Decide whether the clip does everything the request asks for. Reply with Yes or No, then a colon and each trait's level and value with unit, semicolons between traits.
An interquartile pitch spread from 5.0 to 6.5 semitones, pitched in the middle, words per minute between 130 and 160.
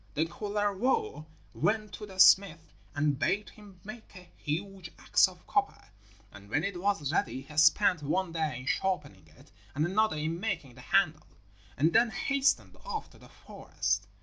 No: wide, 5.4 semitones; medium, 180 Hz; average, 170 wpm